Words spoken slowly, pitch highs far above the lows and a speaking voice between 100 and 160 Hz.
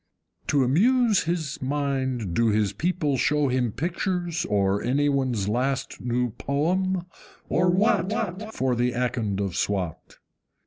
Yes: slow, 130 wpm; wide, 6.6 semitones; medium, 140 Hz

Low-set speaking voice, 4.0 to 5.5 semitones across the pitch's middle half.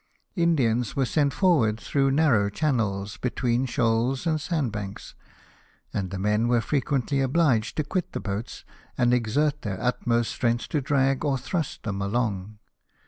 Yes: low, 125 Hz; average, 4.8 semitones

